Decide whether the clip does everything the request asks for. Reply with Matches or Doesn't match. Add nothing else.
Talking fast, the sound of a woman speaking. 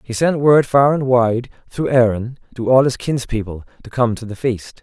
Doesn't match